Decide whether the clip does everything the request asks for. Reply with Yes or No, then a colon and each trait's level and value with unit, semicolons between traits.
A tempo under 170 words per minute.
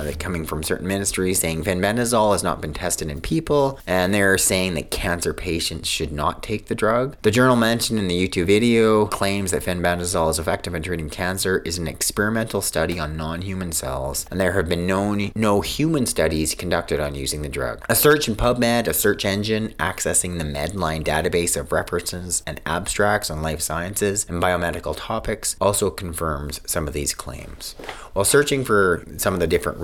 No: average, 185 wpm